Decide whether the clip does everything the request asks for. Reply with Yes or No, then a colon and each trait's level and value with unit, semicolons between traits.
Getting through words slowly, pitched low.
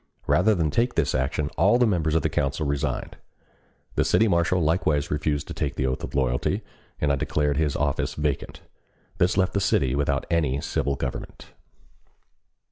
No: average, 175 wpm; very low, 75 Hz